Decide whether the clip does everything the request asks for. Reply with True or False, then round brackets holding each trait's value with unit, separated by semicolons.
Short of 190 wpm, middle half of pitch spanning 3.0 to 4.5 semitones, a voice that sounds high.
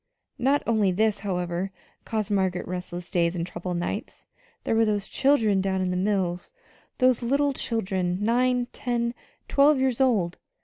False (150 wpm; 5.0 semitones; 205 Hz)